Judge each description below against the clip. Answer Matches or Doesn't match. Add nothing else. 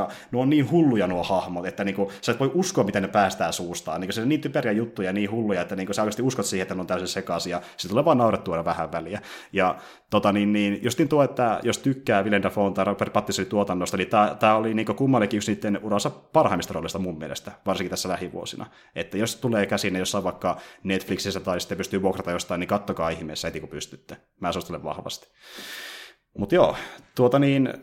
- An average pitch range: Matches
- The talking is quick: Matches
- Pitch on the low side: Matches